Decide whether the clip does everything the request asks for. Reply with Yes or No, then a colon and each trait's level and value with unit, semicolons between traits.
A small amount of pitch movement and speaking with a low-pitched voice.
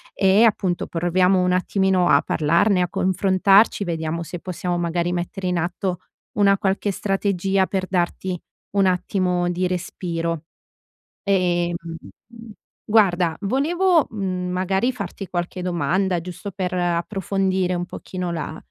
No: narrow, 1.8 semitones; medium, 185 Hz